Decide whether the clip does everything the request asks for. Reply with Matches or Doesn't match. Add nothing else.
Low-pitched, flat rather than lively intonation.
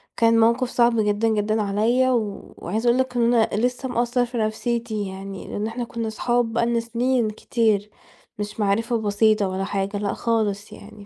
Doesn't match